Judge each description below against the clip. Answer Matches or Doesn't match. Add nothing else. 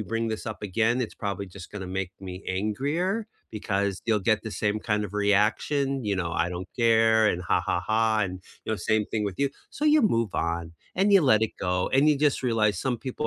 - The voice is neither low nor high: Doesn't match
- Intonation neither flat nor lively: Matches